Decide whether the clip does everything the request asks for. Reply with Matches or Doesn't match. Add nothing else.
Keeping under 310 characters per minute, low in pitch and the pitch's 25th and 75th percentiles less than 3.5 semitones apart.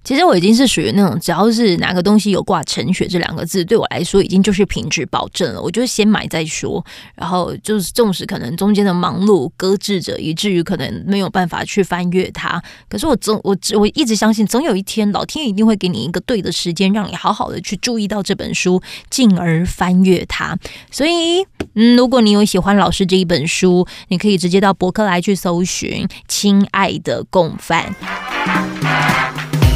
Doesn't match